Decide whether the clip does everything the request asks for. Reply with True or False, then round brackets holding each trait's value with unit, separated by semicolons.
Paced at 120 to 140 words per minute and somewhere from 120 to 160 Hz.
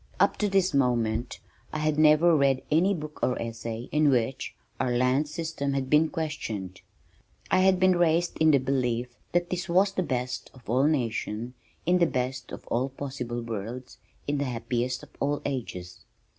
False (175 wpm; 135 Hz)